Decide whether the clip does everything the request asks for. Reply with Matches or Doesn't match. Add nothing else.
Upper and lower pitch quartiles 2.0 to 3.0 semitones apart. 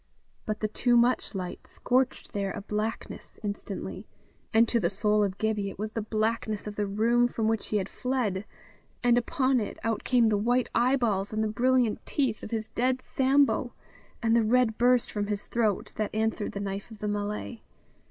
Matches